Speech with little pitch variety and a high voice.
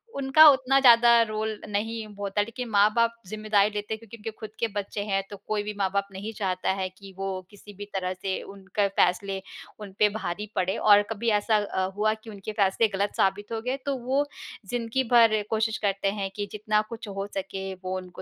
Yes: narrow, 2.2 semitones; high, 210 Hz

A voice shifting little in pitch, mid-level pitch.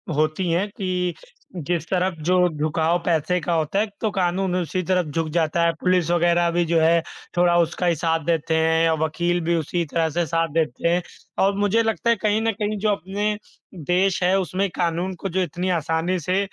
Yes: narrow, 2.3 semitones; medium, 175 Hz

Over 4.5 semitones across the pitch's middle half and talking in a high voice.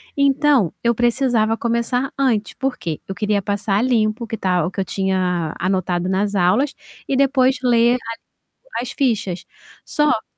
Yes: average, 5.1 semitones; high, 225 Hz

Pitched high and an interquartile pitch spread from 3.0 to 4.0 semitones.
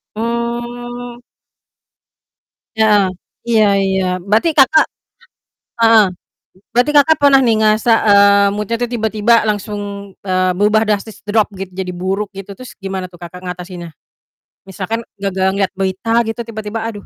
Yes: high, 210 Hz; average, 3.3 semitones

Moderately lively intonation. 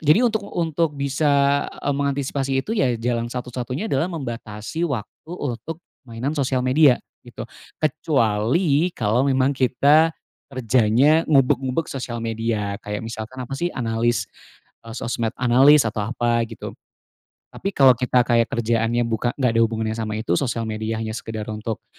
Yes: average, 3.8 semitones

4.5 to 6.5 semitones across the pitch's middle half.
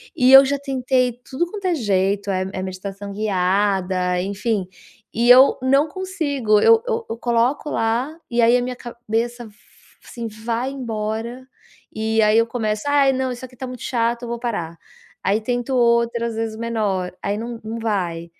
No: average, 3.3 semitones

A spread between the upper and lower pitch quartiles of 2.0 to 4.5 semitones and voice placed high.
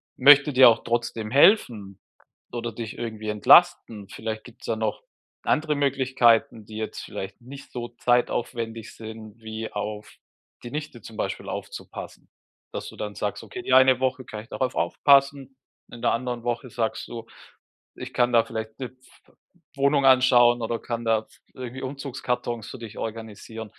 No: average, 2.8 semitones; low, 120 Hz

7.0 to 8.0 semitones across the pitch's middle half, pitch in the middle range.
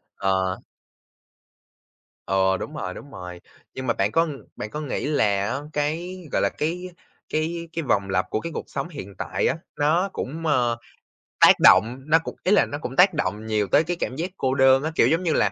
Yes: wide, 7.7 semitones; medium, 145 Hz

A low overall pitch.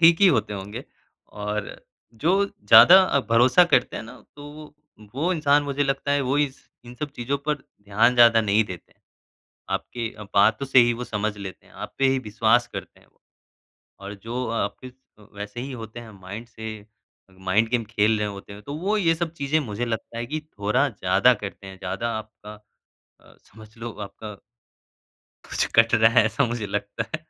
Yes: low, 115 Hz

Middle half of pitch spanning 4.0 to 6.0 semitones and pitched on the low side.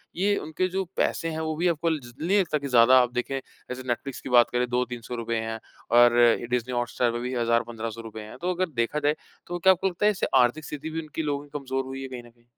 Yes: average, 4.8 semitones; low, 130 Hz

